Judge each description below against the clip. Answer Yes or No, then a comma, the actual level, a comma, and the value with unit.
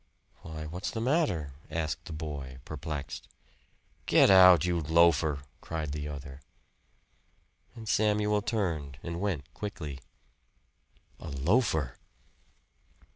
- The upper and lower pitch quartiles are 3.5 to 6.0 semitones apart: Yes, average, 4.8 semitones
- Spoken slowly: Yes, slow, 105 wpm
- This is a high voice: No, very low, 80 Hz